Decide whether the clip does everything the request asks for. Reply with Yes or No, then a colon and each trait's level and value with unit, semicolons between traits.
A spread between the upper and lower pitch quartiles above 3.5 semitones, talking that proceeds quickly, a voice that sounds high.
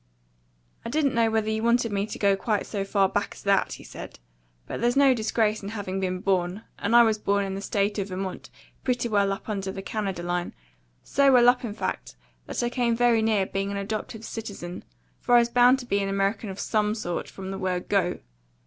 No: average, 3.0 semitones; fast, 225 wpm; high, 205 Hz